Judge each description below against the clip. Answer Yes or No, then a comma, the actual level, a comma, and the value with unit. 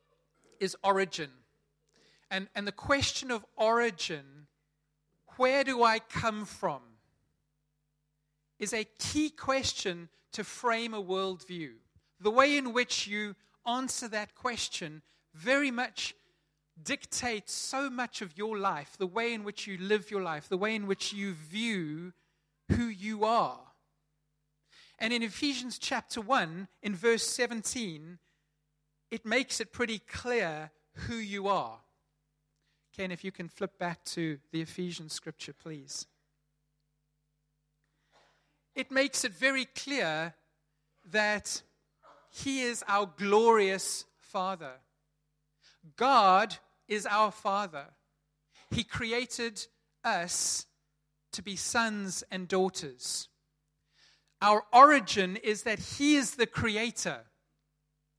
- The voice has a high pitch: Yes, high, 195 Hz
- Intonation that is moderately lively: No, wide, 7.1 semitones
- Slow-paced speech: Yes, slow, 115 wpm